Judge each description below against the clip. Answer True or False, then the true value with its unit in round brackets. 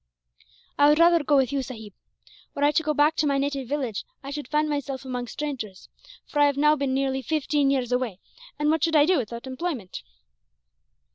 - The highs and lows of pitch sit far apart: False (2.5 semitones)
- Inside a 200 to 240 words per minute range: True (205 wpm)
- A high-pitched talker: True (280 Hz)